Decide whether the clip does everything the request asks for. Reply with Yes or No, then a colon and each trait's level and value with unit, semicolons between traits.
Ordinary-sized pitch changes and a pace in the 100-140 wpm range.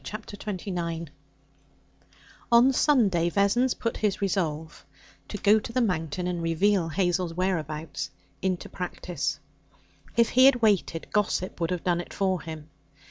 Yes: average, 3.9 semitones; slow, 135 wpm